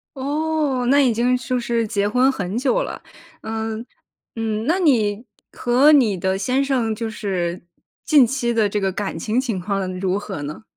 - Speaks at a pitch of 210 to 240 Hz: Yes, high, 230 Hz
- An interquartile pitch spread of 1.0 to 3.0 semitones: No, average, 4.4 semitones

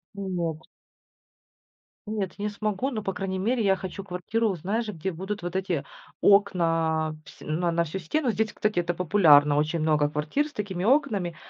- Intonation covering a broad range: No, average, 4.1 semitones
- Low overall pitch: No, high, 190 Hz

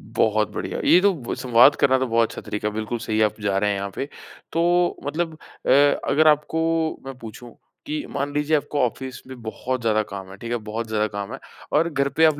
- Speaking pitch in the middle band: No, low, 130 Hz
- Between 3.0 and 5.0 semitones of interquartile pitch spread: No, wide, 5.6 semitones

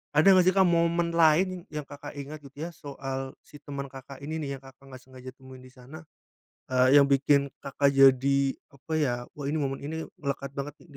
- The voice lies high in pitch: No, medium, 140 Hz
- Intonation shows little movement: Yes, narrow, 2.3 semitones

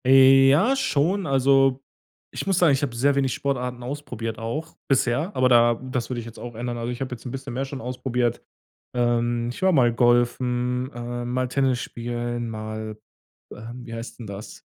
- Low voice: Yes, low, 125 Hz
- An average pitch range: No, narrow, 2.2 semitones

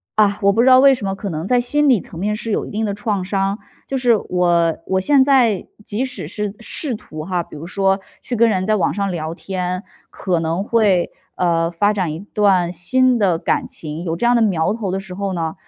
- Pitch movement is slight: No, average, 4.0 semitones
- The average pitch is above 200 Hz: No, high, 195 Hz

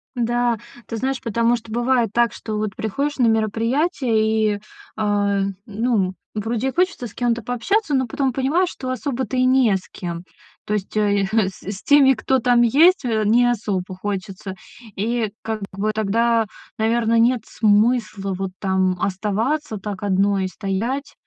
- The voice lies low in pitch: No, high, 225 Hz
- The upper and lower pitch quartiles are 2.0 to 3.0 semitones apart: No, average, 3.4 semitones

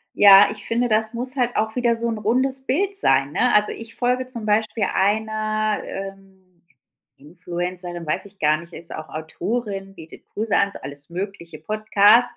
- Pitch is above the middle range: Yes, high, 210 Hz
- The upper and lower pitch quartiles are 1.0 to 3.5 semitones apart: No, average, 4.4 semitones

